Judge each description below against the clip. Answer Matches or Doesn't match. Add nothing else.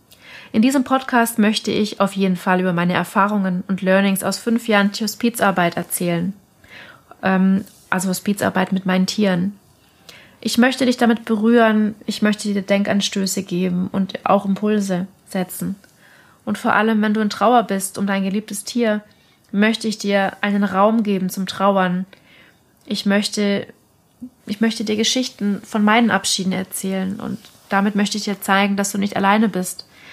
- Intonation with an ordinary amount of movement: Doesn't match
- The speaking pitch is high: Matches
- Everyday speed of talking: Matches